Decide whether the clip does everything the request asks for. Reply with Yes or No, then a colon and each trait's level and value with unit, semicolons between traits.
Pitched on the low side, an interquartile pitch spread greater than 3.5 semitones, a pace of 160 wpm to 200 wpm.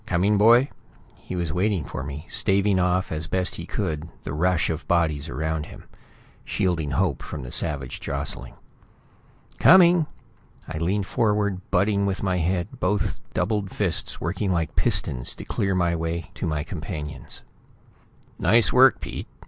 No: very low, 90 Hz; average, 4.0 semitones; average, 150 wpm